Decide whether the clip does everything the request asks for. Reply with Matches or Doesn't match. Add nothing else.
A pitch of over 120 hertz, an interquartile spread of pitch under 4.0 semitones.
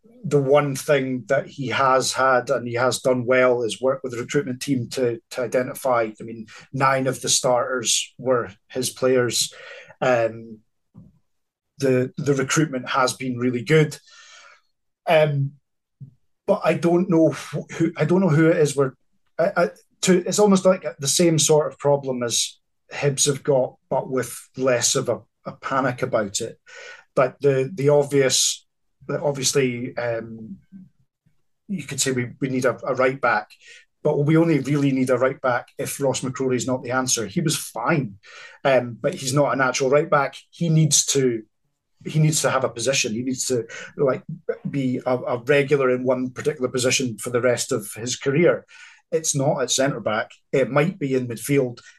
Matches